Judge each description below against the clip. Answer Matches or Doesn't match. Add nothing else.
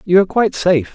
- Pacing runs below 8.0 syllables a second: Doesn't match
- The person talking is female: Doesn't match